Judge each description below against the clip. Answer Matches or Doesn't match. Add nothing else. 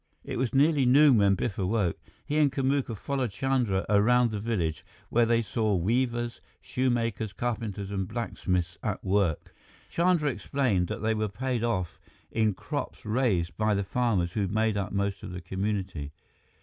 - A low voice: Matches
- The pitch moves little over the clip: Doesn't match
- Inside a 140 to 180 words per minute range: Matches